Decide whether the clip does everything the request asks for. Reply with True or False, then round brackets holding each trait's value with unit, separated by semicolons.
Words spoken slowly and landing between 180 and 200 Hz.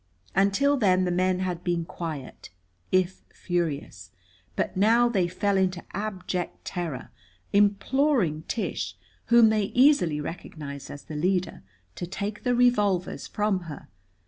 True (130 wpm; 185 Hz)